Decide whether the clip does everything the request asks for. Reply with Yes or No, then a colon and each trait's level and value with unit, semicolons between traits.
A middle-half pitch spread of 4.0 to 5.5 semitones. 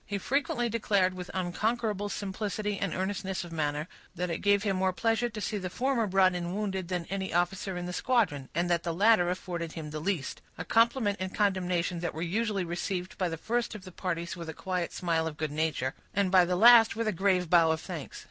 No: average, 3.1 semitones